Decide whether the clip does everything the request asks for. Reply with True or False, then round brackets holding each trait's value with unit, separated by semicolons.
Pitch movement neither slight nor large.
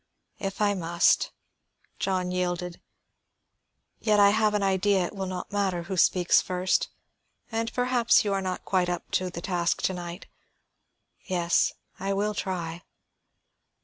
False (2.2 semitones)